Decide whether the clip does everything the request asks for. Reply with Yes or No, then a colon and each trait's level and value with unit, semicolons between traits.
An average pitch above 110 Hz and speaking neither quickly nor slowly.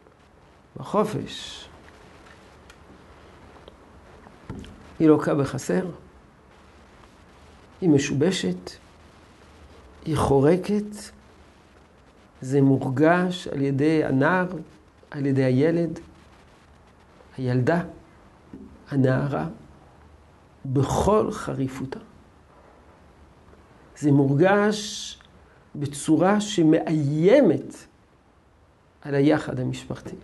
No: medium, 140 Hz; slow, 55 wpm